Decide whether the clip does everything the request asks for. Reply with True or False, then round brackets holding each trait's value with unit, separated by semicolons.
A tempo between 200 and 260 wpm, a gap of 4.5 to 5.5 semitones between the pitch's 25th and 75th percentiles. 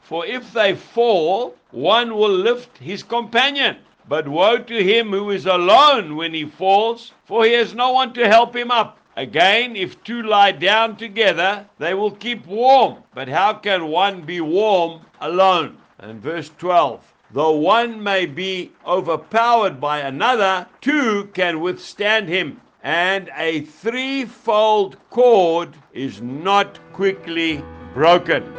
False (140 wpm; 5.2 semitones)